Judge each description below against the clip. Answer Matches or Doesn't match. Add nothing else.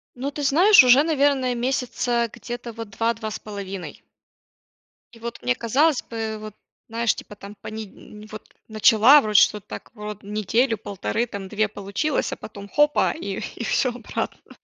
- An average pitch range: Matches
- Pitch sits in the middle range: Doesn't match